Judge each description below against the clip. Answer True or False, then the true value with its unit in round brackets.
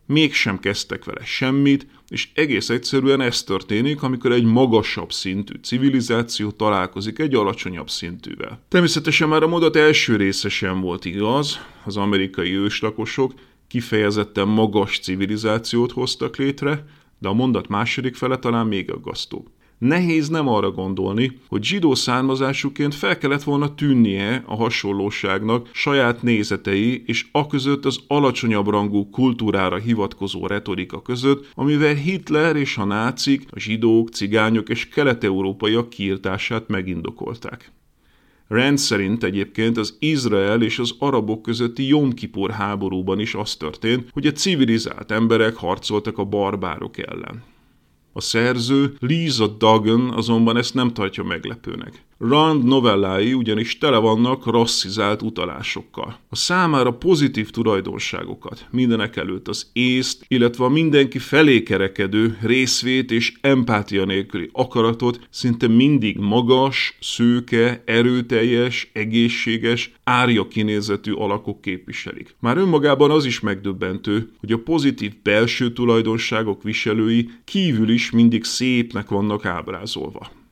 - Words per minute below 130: True (120 wpm)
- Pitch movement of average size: True (4.0 semitones)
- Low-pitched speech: True (115 Hz)